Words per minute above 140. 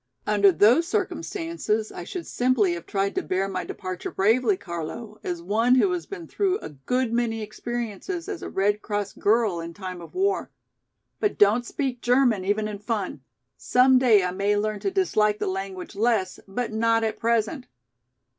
Yes: average, 175 wpm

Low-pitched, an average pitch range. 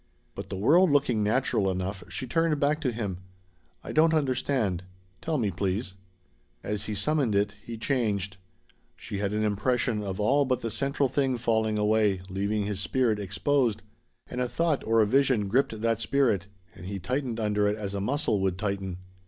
Yes: low, 110 Hz; average, 4.6 semitones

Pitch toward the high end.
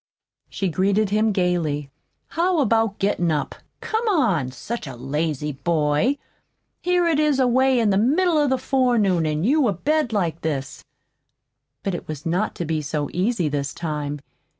Yes: high, 195 Hz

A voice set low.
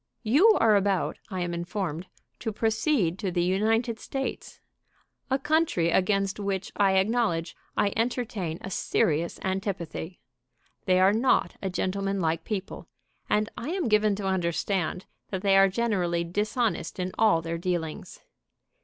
No: high, 195 Hz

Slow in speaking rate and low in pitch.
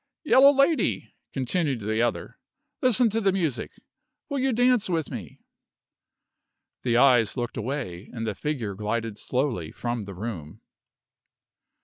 Yes: slow, 130 wpm; low, 125 Hz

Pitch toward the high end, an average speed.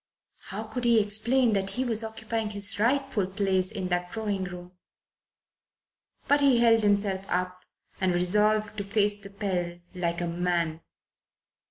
Yes: high, 205 Hz; average, 150 wpm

